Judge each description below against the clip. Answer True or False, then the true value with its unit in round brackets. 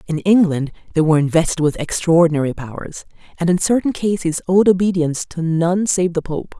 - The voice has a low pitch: False (170 Hz)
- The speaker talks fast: False (175 wpm)